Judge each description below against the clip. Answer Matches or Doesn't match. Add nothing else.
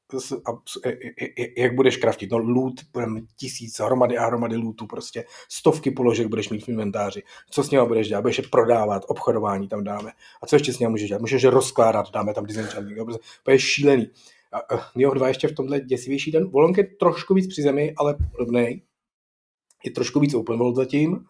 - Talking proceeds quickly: Matches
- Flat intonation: Doesn't match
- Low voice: Matches